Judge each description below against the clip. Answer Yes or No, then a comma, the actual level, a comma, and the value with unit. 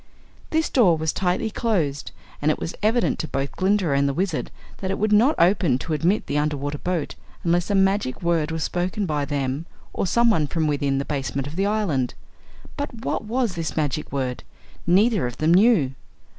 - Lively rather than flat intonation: Yes, wide, 5.9 semitones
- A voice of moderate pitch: Yes, medium, 170 Hz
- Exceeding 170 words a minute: Yes, average, 190 wpm